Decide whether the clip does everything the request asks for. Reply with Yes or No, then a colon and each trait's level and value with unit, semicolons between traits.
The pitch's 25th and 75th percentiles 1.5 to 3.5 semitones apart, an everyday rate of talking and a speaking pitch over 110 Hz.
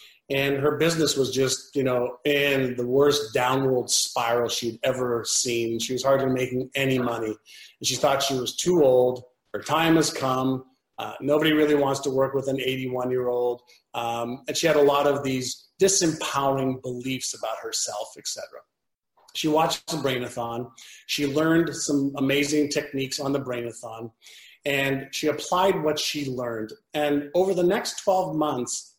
Yes: average, 2.8 semitones; average, 160 wpm; low, 135 Hz